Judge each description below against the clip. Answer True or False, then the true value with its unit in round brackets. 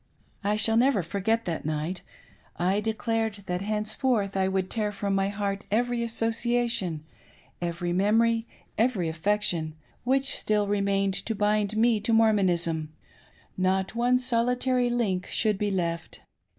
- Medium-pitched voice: False (210 Hz)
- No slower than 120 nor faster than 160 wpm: True (150 wpm)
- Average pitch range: True (3.3 semitones)